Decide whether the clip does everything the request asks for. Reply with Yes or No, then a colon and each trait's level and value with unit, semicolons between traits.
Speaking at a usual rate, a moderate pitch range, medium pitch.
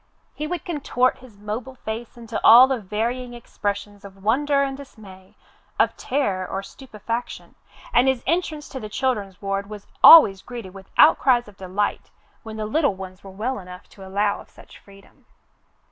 No: average, 170 wpm; average, 4.7 semitones; high, 220 Hz